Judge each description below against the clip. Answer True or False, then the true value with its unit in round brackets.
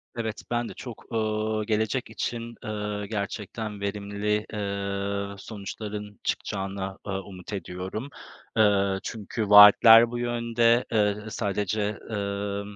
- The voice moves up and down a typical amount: False (1.7 semitones)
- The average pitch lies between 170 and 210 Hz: False (105 Hz)